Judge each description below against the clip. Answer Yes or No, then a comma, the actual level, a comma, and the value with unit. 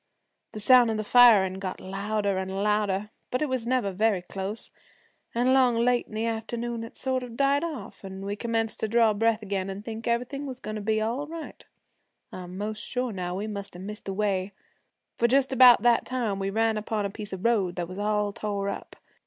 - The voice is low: No, high, 215 Hz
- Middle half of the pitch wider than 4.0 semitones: No, average, 3.2 semitones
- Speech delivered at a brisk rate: Yes, fast, 215 wpm